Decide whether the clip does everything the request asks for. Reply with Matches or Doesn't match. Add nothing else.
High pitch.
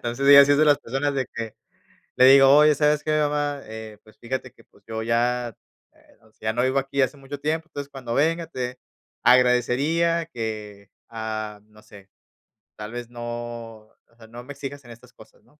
Doesn't match